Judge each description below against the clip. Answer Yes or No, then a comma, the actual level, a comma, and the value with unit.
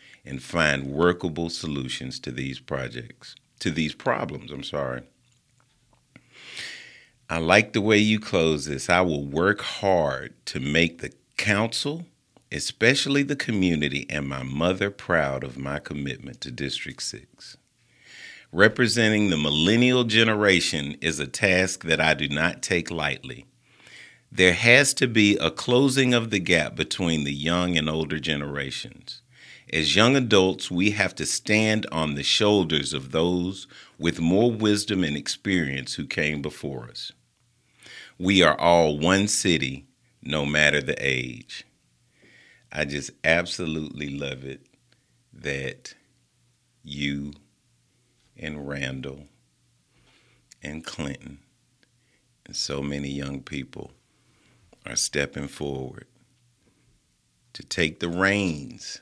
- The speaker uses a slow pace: Yes, slow, 125 wpm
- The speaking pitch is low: Yes, very low, 80 Hz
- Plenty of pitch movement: Yes, wide, 6.9 semitones